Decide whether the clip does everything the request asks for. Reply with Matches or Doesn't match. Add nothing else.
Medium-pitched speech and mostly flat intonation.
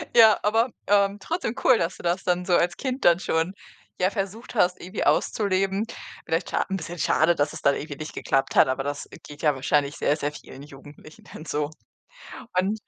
Doesn't match